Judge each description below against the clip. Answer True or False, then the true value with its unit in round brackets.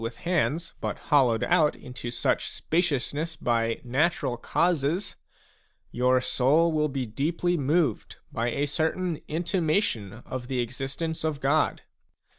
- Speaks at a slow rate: True (125 wpm)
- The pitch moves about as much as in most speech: True (4.7 semitones)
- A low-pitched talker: False (145 Hz)